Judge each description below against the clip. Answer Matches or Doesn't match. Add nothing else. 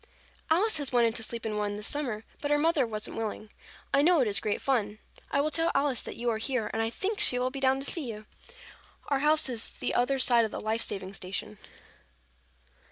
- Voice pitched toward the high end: Matches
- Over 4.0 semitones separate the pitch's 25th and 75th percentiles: Matches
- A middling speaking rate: Doesn't match